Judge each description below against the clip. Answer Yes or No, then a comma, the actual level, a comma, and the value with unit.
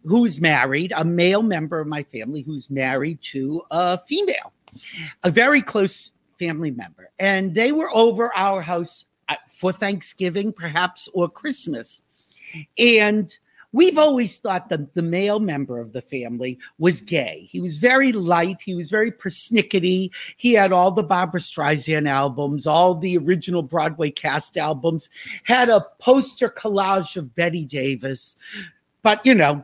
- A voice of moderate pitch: Yes, medium, 180 Hz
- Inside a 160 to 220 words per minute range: No, average, 150 wpm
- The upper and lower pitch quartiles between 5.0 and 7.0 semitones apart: Yes, average, 5.3 semitones